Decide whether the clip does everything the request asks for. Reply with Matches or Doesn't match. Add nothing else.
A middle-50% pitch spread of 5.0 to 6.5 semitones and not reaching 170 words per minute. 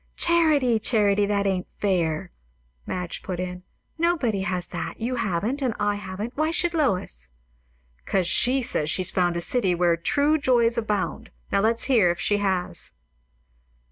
Matches